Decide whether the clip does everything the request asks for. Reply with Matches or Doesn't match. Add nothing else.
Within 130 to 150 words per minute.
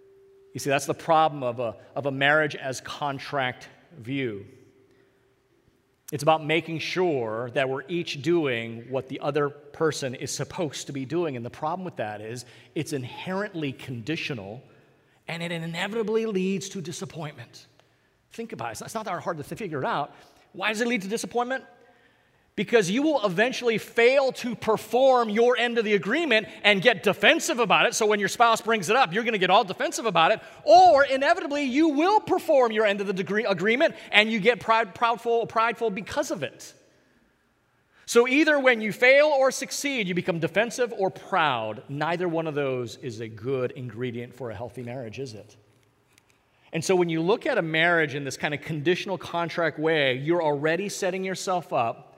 Doesn't match